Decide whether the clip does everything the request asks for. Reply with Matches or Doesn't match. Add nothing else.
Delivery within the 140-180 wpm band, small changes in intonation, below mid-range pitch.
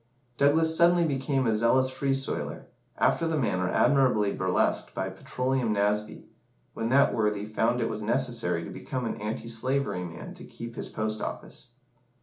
Doesn't match